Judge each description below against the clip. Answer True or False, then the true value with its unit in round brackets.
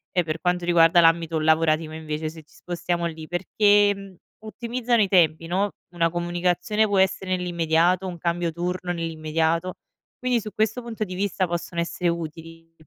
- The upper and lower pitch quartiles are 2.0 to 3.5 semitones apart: True (2.5 semitones)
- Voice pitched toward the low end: False (175 Hz)